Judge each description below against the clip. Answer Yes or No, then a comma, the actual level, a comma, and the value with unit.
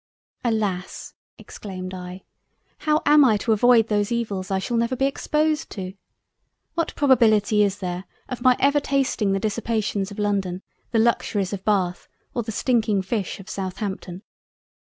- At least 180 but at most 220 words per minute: No, average, 150 wpm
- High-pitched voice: Yes, high, 210 Hz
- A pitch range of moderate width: Yes, average, 4.0 semitones